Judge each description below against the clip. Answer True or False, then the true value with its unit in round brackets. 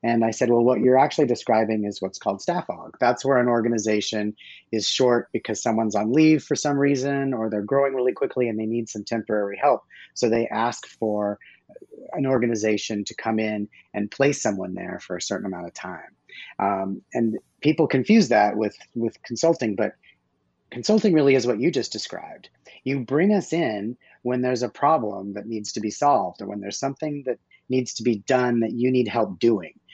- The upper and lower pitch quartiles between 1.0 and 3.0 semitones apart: False (3.7 semitones)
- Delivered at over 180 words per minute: True (200 wpm)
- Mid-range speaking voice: False (115 Hz)